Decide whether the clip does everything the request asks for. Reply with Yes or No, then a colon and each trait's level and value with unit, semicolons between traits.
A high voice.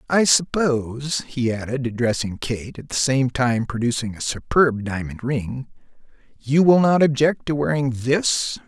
No: low, 130 Hz